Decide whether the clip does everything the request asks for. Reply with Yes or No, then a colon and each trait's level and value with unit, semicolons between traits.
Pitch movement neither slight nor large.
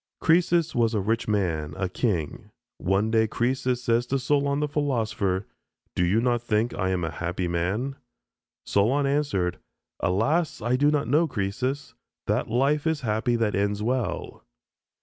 No: wide, 5.8 semitones